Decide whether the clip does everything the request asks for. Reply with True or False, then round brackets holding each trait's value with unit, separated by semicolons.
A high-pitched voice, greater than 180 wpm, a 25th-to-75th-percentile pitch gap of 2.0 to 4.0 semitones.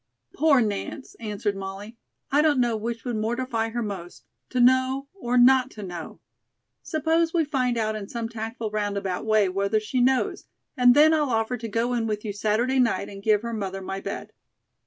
True (230 Hz; 190 wpm; 3.5 semitones)